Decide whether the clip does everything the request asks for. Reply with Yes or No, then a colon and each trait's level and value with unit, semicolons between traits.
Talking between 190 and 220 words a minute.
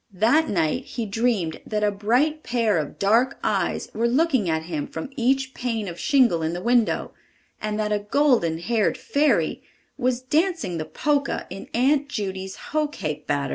No: average, 175 wpm